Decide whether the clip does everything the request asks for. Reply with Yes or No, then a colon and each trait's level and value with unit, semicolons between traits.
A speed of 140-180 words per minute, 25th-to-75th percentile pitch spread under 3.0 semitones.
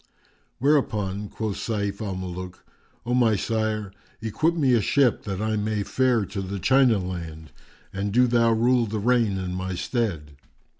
No: average, 160 wpm; average, 3.8 semitones